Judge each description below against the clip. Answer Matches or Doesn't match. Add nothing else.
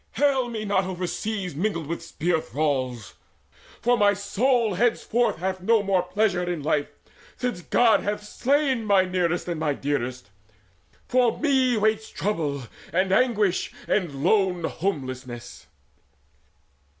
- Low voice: Doesn't match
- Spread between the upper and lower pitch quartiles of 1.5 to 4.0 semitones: Doesn't match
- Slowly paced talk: Matches